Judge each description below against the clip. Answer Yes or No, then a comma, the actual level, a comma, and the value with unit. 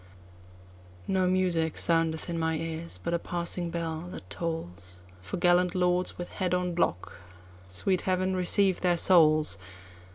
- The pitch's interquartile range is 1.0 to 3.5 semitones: Yes, narrow, 2.6 semitones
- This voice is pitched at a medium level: Yes, medium, 170 Hz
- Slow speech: Yes, slow, 130 wpm